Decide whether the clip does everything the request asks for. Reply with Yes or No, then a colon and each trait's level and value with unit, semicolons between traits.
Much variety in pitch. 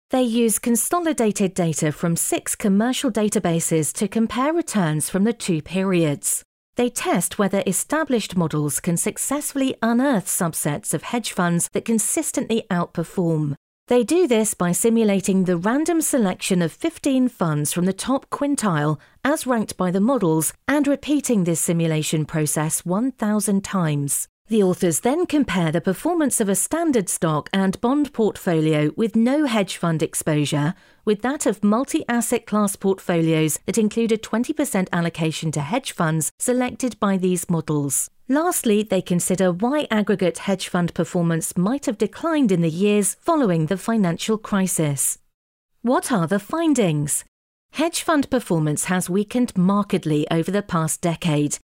Yes: wide, 6.4 semitones